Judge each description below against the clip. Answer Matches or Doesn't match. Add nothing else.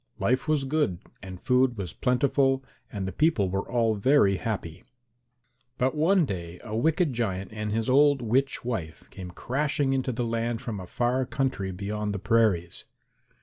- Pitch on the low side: Matches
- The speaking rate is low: Doesn't match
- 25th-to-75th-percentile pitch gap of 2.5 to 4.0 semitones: Doesn't match